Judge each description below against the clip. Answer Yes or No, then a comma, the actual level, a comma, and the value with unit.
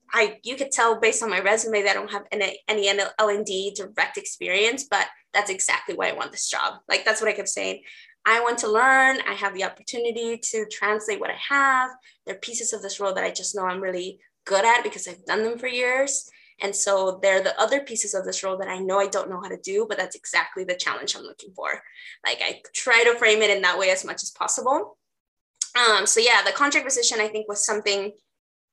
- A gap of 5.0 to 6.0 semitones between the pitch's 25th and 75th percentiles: No, average, 4.1 semitones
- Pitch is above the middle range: Yes, high, 215 Hz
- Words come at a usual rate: No, fast, 240 wpm